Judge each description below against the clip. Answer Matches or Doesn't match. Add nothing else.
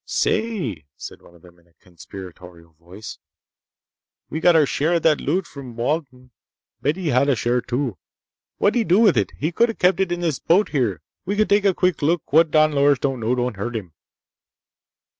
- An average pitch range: Doesn't match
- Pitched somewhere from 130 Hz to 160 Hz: Matches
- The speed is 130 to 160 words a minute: Doesn't match